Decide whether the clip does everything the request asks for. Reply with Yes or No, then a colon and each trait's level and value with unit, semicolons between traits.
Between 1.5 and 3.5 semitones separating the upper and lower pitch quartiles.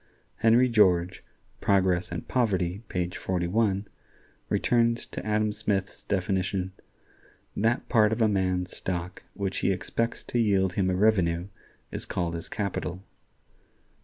Yes: average, 2.9 semitones